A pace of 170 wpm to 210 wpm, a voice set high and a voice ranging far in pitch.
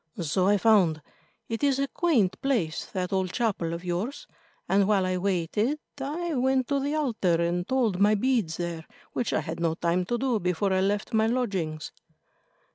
Yes: average, 185 wpm; high, 200 Hz; wide, 6.1 semitones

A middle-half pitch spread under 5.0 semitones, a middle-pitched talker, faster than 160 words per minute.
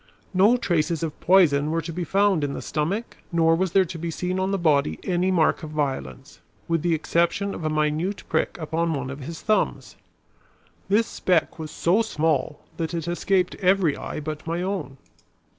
Yes: average, 3.4 semitones; medium, 165 Hz; average, 190 wpm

